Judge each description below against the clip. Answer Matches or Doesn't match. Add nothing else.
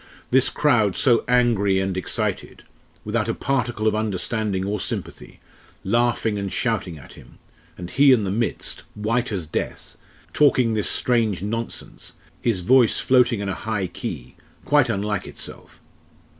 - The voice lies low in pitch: Matches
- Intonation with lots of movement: Doesn't match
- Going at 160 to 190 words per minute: Doesn't match